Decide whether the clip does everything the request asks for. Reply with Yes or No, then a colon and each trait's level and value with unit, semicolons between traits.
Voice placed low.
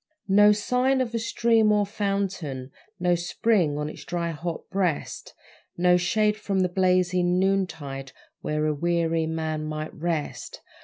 No: medium, 180 Hz